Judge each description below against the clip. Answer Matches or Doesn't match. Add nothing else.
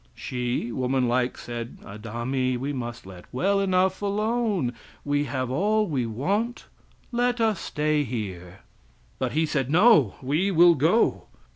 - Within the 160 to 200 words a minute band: Doesn't match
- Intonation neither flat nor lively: Doesn't match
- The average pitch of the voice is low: Doesn't match